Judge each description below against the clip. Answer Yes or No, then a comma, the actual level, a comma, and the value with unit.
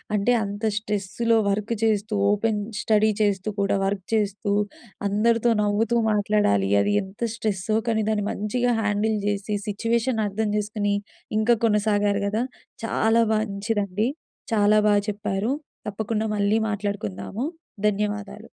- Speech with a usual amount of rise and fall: No, narrow, 1.5 semitones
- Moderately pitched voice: No, high, 210 Hz